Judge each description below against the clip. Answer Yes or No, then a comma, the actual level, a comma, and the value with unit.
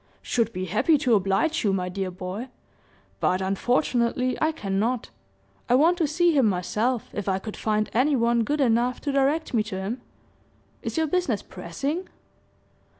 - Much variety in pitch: Yes, wide, 6.4 semitones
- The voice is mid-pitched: No, high, 235 Hz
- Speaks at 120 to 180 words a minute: Yes, average, 165 wpm